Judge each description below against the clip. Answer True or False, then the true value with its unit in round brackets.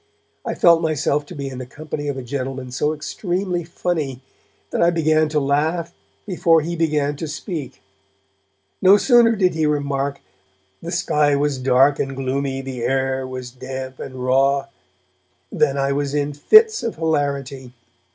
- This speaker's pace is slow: False (160 wpm)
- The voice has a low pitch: False (145 Hz)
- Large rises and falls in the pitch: False (3.3 semitones)